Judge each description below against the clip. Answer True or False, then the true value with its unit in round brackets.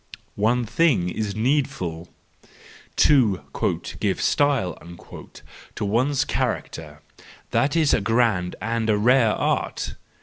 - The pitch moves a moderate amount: False (6.2 semitones)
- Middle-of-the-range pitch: False (110 Hz)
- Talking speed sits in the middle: False (100 wpm)